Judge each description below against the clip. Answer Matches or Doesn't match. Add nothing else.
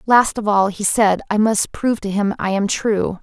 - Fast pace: Matches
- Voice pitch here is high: Matches